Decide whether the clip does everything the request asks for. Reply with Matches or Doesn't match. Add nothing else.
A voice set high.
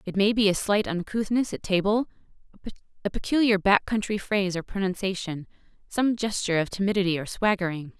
Matches